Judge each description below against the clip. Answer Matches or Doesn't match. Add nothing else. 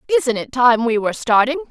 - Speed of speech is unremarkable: Doesn't match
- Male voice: Doesn't match